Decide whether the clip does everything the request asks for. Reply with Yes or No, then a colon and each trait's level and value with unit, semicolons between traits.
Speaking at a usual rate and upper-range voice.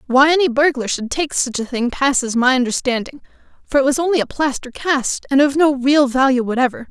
No: fast, 210 wpm; very high, 270 Hz